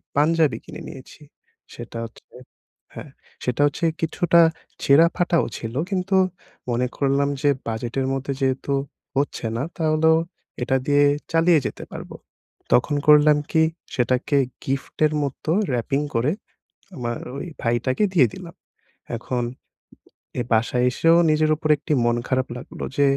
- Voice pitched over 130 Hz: Yes, medium, 140 Hz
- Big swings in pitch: No, average, 3.8 semitones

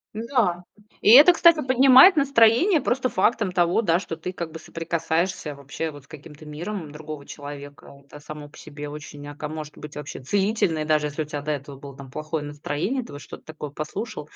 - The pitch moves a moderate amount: No, wide, 6.0 semitones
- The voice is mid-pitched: Yes, medium, 155 Hz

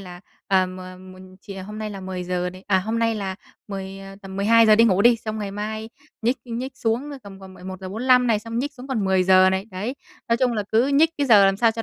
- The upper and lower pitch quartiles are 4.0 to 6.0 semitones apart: No, average, 3.4 semitones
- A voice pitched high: Yes, high, 210 Hz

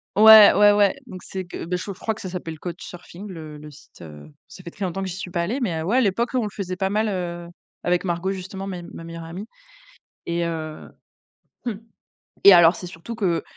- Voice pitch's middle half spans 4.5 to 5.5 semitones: No, average, 2.8 semitones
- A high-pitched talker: No, medium, 180 Hz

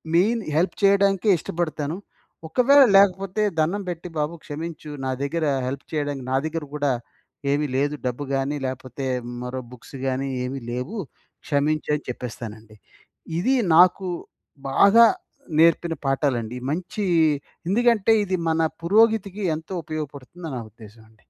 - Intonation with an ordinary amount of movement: No, wide, 5.8 semitones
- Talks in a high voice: No, medium, 155 Hz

